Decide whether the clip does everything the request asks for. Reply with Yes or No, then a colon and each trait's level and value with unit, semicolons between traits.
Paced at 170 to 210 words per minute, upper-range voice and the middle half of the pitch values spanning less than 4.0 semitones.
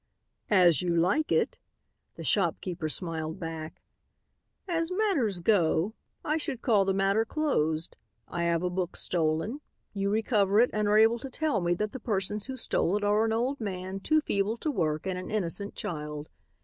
No: average, 175 wpm; high, 200 Hz; average, 4.7 semitones